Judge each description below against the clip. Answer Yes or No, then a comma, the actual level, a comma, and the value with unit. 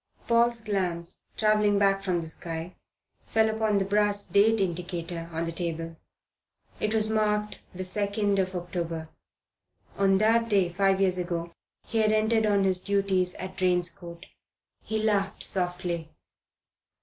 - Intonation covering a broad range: No, average, 3.2 semitones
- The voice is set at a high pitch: Yes, high, 195 Hz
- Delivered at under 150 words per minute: Yes, average, 140 wpm